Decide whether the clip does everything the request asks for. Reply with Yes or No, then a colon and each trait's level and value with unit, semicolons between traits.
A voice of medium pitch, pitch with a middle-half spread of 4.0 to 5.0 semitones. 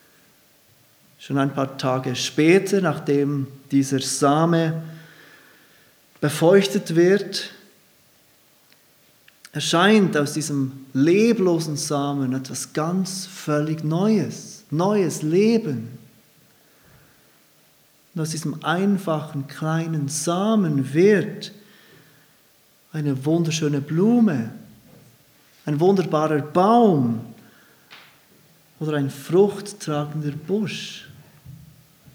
Yes: medium, 155 Hz; average, 4.7 semitones